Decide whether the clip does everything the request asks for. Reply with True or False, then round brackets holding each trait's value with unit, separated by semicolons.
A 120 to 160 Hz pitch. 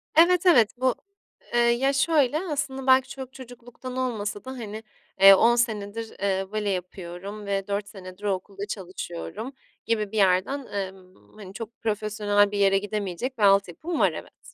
False (215 Hz)